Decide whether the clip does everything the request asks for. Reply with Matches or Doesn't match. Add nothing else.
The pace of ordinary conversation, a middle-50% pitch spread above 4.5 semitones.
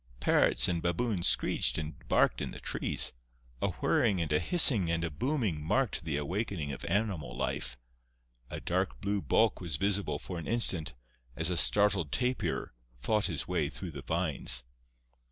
Matches